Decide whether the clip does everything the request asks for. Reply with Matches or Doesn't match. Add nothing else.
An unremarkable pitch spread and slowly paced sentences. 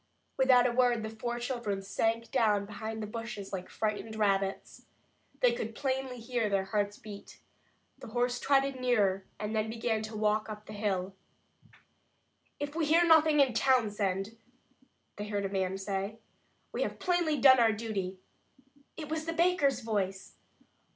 Doesn't match